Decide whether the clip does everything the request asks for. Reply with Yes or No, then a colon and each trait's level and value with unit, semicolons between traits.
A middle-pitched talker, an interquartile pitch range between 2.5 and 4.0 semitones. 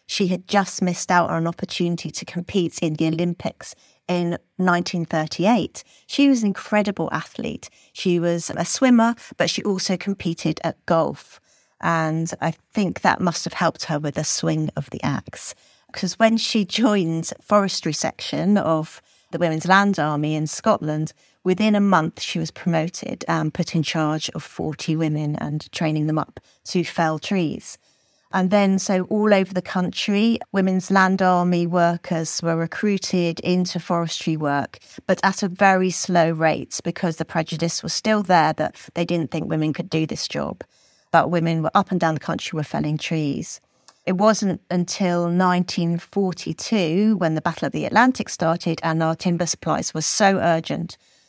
Yes: medium, 175 Hz; average, 3.1 semitones